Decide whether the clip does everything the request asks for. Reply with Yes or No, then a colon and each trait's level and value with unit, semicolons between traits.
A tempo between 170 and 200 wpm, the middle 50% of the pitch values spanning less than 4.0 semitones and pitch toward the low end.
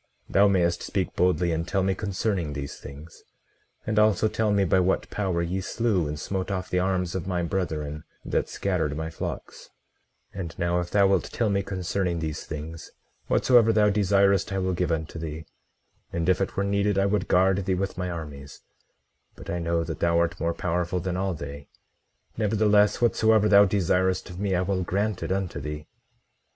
Yes: average, 190 wpm; average, 2.8 semitones; very low, 95 Hz